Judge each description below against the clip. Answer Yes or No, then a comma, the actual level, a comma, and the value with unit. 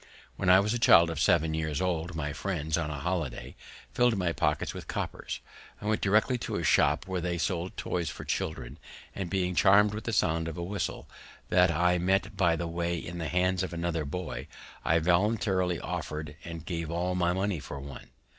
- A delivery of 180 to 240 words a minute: Yes, average, 200 wpm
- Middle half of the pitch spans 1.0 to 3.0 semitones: Yes, narrow, 2.5 semitones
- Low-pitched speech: Yes, very low, 85 Hz